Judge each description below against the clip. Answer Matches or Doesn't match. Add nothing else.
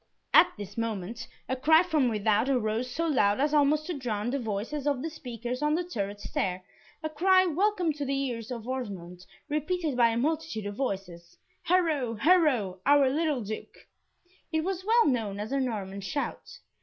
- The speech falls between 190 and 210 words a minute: Doesn't match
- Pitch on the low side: Doesn't match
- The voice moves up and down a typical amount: Doesn't match